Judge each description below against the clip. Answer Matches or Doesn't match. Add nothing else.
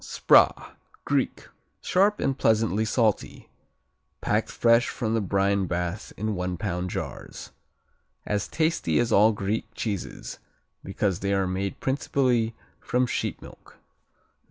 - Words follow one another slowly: Matches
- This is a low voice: Matches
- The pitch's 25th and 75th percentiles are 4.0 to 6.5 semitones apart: Doesn't match